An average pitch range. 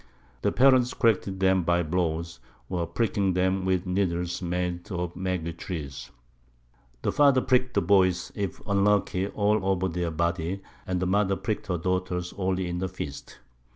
No: narrow, 2.0 semitones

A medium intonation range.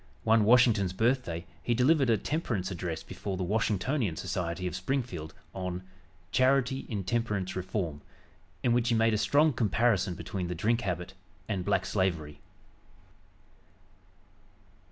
Yes: average, 4.7 semitones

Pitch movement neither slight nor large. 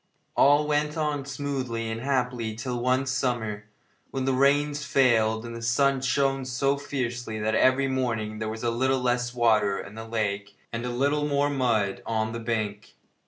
Yes: average, 3.4 semitones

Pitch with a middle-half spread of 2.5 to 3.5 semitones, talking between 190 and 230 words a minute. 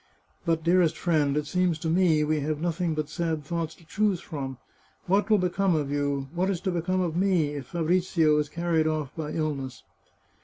Yes: average, 2.9 semitones; fast, 205 wpm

